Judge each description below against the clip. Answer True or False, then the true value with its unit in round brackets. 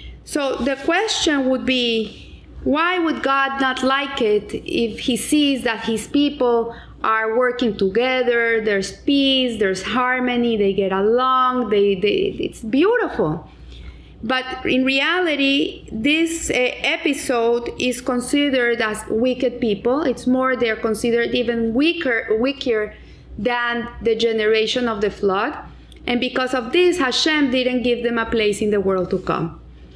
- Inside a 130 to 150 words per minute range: True (140 wpm)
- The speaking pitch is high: True (250 Hz)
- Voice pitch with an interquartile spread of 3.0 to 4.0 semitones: True (3.3 semitones)